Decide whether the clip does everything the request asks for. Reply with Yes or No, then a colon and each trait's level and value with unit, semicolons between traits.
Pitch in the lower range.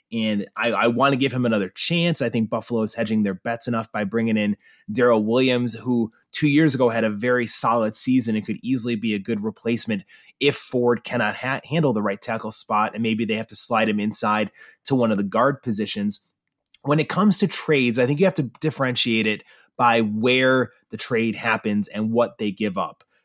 Yes: low, 115 Hz